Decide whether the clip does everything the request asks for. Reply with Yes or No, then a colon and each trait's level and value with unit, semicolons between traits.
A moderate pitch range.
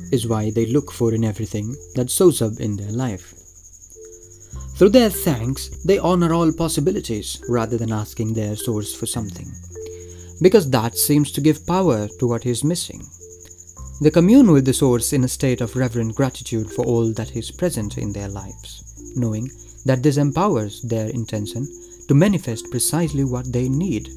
Yes: average, 4.9 semitones